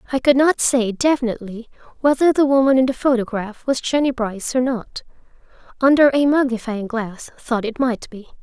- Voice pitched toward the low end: No, very high, 250 Hz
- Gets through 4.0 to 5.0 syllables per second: No, 5.4 syllables/s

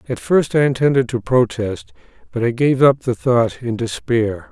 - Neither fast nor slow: Yes, average, 185 wpm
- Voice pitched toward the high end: No, low, 125 Hz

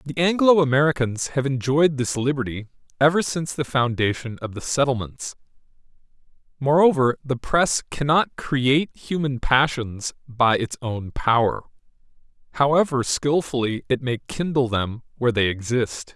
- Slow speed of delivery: Yes, slow, 125 wpm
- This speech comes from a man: Yes, male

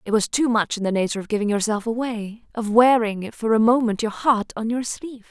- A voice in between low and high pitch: No, high, 225 Hz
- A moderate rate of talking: No, fast, 225 wpm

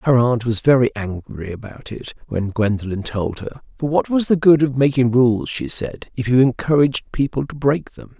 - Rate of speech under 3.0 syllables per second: No, 4.9 syllables/s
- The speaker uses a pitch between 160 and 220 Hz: No, low, 125 Hz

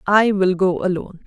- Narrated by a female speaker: Yes, female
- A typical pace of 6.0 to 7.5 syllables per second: No, 5.5 syllables/s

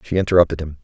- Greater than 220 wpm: No, fast, 215 wpm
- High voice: No, very low, 85 Hz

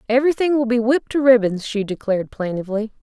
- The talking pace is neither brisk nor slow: Yes, average, 175 wpm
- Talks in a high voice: Yes, high, 235 Hz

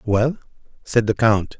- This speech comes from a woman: No, male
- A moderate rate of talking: Yes, average, 150 wpm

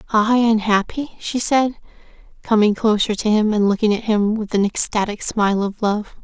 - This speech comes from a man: No, female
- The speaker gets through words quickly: No, average, 175 wpm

